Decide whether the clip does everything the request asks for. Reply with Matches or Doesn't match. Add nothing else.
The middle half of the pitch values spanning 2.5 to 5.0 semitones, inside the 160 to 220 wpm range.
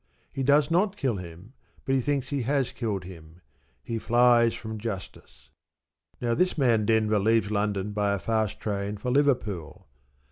Matches